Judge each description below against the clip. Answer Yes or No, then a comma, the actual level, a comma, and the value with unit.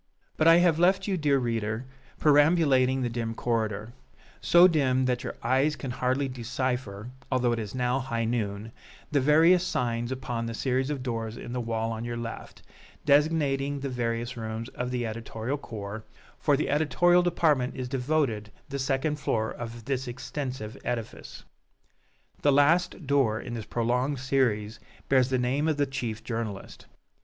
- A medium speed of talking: Yes, average, 165 wpm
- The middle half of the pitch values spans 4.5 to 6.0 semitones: No, average, 3.6 semitones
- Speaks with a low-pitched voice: Yes, low, 125 Hz